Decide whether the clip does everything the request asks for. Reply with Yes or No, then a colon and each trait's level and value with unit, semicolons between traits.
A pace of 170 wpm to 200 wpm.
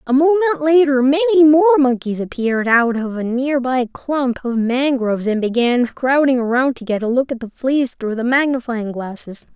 Yes: average, 190 wpm